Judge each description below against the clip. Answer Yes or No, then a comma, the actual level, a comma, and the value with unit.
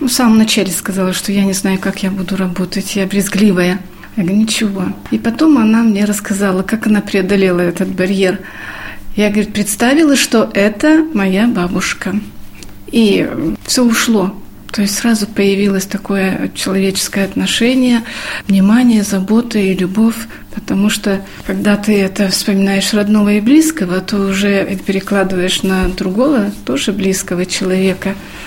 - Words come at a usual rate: Yes, average, 140 wpm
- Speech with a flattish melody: Yes, narrow, 2.3 semitones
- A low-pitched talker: No, high, 200 Hz